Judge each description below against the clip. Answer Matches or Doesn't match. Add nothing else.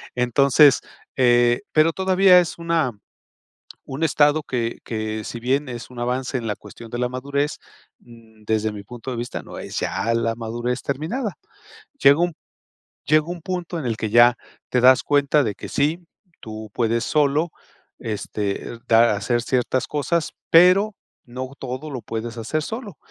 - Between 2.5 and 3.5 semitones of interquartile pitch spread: Doesn't match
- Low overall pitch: Matches